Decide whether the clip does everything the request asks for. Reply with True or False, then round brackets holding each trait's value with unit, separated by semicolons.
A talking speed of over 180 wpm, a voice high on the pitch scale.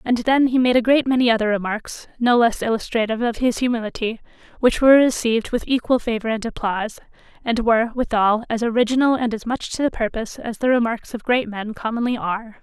True (200 wpm; 235 Hz)